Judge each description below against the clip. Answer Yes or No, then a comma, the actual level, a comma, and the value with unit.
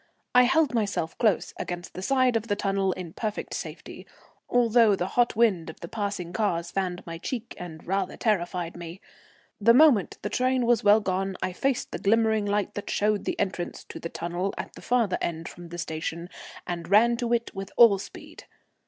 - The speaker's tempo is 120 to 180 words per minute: No, average, 195 wpm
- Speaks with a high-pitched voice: Yes, high, 200 Hz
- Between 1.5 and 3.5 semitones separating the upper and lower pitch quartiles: No, average, 4.7 semitones